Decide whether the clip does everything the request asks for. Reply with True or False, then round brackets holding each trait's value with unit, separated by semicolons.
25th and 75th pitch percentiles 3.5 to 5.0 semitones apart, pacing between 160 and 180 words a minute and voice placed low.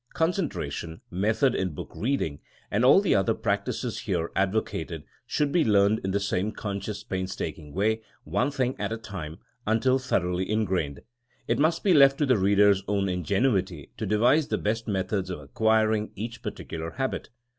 True (4.5 semitones; 170 wpm; 105 Hz)